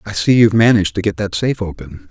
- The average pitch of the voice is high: No, low, 105 Hz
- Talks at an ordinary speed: No, fast, 255 wpm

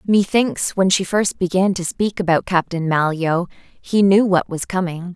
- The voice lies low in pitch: No, medium, 185 Hz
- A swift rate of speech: No, average, 175 wpm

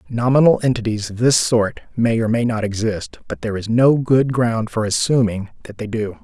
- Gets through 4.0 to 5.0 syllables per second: No, 5.2 syllables/s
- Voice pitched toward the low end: Yes, low, 115 Hz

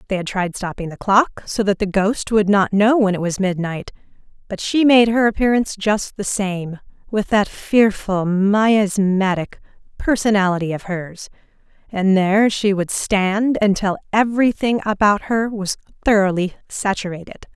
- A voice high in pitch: Yes, high, 200 Hz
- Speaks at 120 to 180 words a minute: Yes, average, 150 wpm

